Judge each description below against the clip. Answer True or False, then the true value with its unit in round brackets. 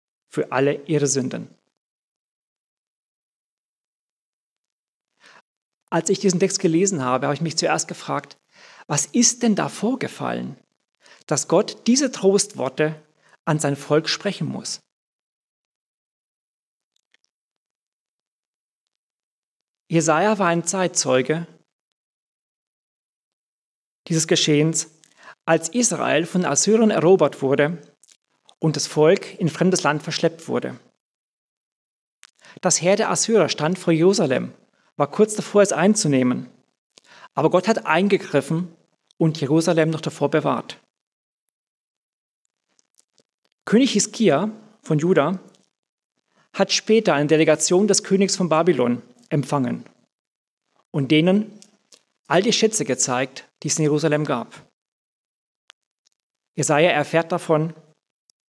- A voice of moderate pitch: True (165 Hz)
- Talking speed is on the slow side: True (100 wpm)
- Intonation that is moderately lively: True (4.5 semitones)